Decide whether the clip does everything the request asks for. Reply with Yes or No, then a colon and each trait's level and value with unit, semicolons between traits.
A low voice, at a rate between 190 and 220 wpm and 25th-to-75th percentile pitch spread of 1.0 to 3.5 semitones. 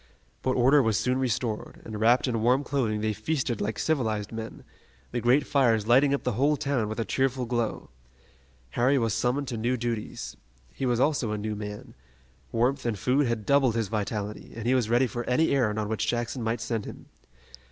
Yes: low, 120 Hz; average, 200 wpm; average, 3.1 semitones